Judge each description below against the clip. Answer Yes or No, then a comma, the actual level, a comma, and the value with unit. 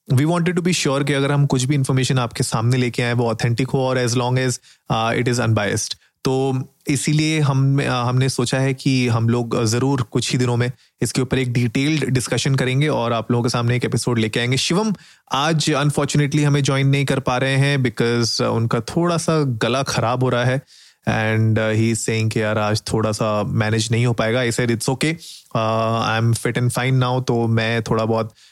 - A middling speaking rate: No, fast, 210 wpm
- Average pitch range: Yes, average, 3.0 semitones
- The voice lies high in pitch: No, low, 125 Hz